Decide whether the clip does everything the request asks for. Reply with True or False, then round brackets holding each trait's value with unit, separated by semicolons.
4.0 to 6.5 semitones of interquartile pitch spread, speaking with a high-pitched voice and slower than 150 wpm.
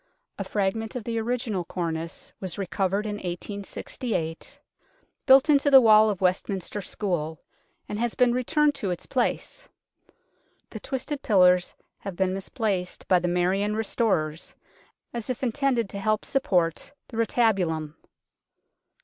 True (4.6 semitones; 205 Hz; 135 wpm)